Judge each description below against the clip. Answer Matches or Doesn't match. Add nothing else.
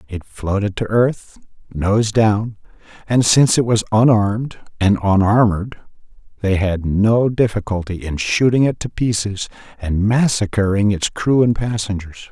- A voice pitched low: Matches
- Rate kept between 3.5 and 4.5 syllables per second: Matches